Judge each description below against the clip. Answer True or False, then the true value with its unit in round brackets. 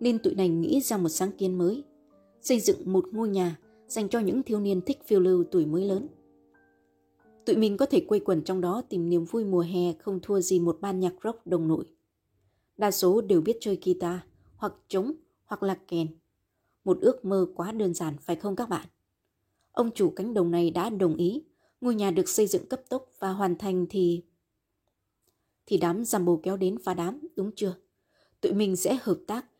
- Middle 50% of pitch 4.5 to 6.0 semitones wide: False (3.7 semitones)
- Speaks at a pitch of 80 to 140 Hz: False (185 Hz)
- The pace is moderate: True (205 wpm)